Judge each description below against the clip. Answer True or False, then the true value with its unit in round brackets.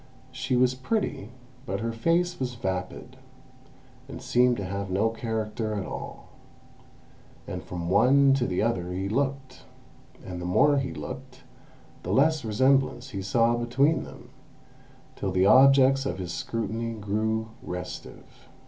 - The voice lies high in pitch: False (115 Hz)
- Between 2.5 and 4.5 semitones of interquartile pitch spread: False (5.0 semitones)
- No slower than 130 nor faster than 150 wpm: True (140 wpm)